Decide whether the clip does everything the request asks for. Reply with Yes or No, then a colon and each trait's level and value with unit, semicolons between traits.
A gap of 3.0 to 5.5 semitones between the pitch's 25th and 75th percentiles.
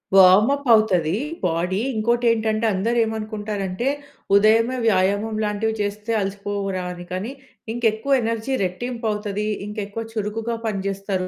No: narrow, 2.4 semitones